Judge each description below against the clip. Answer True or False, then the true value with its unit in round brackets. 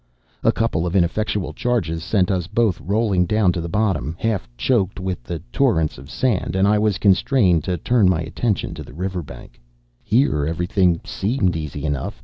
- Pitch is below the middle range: True (95 Hz)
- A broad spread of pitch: False (4.3 semitones)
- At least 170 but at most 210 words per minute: True (180 wpm)